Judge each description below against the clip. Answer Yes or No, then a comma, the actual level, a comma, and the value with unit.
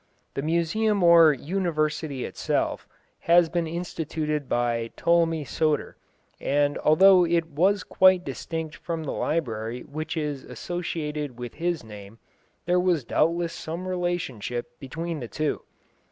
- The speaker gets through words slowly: Yes, slow, 125 wpm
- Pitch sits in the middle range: Yes, medium, 160 Hz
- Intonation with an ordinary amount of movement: Yes, average, 3.2 semitones